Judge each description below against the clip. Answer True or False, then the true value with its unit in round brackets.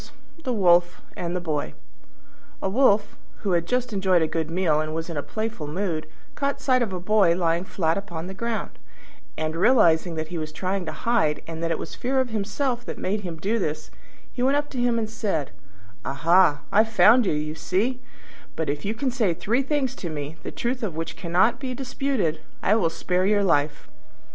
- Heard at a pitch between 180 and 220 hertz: True (185 Hz)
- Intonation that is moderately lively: False (6.2 semitones)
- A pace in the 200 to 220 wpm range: True (205 wpm)